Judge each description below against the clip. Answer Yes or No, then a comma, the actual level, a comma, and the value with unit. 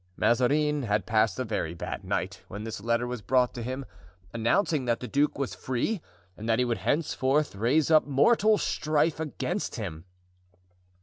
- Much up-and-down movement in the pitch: No, average, 4.6 semitones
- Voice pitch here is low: Yes, low, 125 Hz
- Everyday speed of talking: Yes, average, 170 wpm